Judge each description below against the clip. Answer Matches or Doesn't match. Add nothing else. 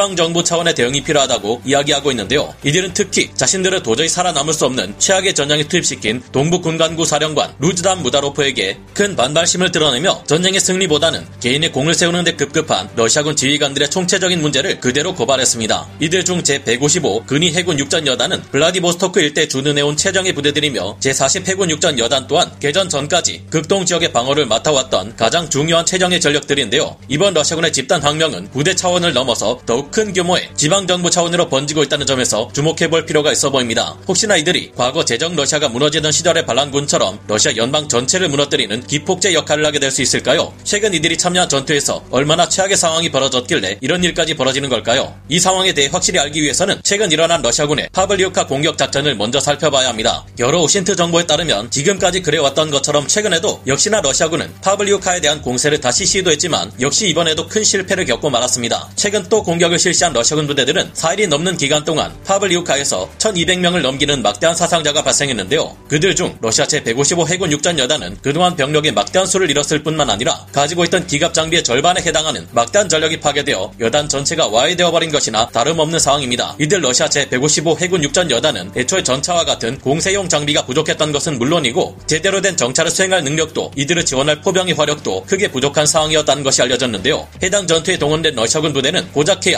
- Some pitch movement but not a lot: Matches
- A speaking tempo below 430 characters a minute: Doesn't match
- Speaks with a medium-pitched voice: Matches